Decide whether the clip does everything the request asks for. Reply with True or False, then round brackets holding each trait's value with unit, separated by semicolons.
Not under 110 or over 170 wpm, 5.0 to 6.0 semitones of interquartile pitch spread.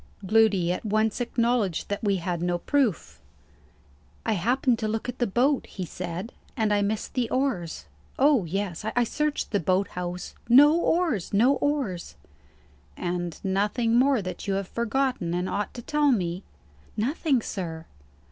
True (155 wpm; 5.4 semitones)